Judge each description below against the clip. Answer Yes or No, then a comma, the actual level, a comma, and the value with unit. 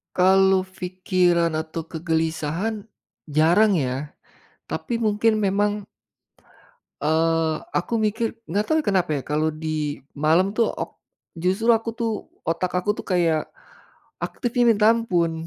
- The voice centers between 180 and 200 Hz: Yes, medium, 185 Hz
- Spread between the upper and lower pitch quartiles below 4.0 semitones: No, average, 4.4 semitones